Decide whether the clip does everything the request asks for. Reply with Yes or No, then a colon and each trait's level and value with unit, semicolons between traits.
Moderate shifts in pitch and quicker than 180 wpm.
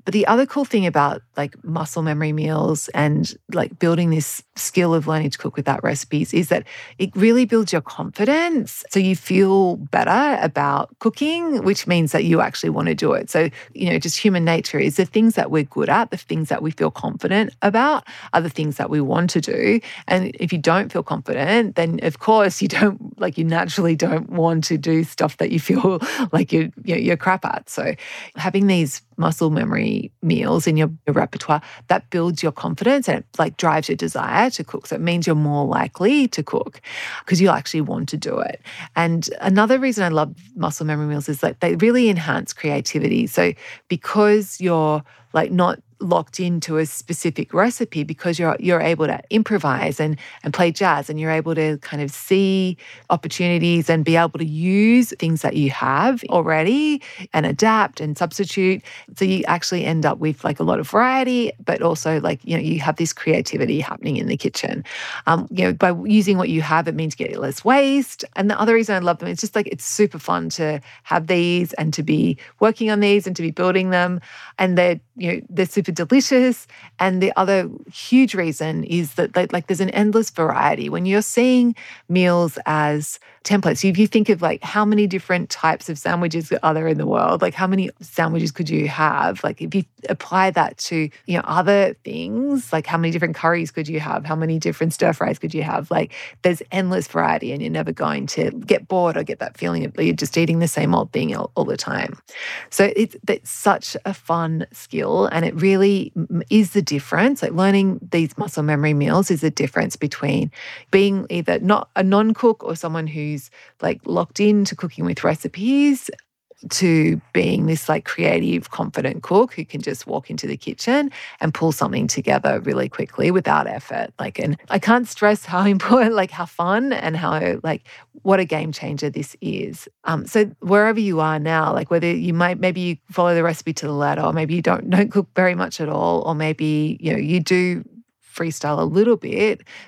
Yes: average, 4.2 semitones; fast, 205 wpm